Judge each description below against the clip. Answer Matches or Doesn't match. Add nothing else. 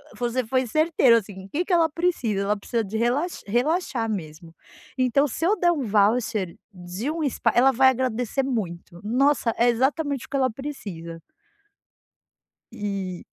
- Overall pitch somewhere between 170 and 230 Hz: Doesn't match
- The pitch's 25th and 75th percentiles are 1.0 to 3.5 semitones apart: Doesn't match